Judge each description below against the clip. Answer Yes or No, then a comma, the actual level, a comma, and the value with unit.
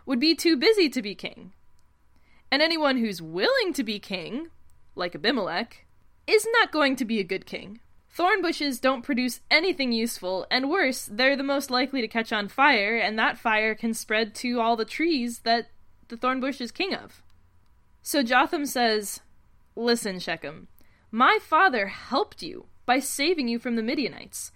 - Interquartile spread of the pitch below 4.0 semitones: No, average, 4.6 semitones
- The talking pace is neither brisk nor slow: Yes, average, 170 wpm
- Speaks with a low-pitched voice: No, very high, 250 Hz